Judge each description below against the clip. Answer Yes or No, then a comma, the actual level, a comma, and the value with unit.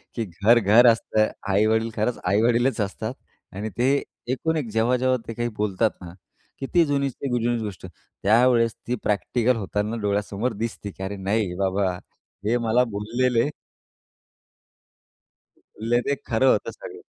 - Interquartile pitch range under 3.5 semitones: Yes, average, 3.1 semitones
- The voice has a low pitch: Yes, low, 115 Hz